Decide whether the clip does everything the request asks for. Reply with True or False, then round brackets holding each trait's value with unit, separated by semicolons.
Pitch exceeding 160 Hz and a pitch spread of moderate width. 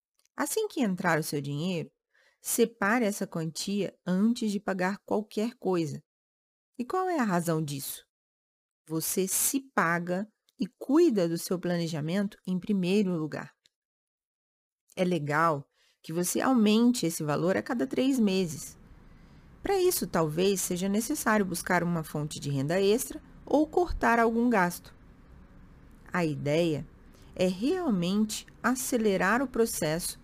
False (185 Hz; 6.1 semitones)